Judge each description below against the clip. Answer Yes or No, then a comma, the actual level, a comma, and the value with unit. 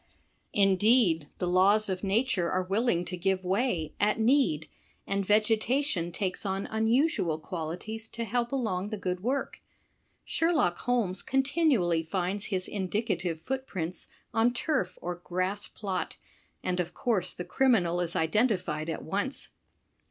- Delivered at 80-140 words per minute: Yes, slow, 135 wpm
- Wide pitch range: No, average, 4.6 semitones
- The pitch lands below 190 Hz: No, high, 195 Hz